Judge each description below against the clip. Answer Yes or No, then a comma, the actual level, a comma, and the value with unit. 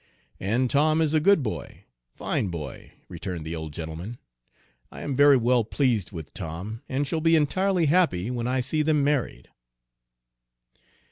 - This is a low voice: Yes, low, 125 Hz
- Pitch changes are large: Yes, wide, 8.7 semitones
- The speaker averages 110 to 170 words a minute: Yes, average, 160 wpm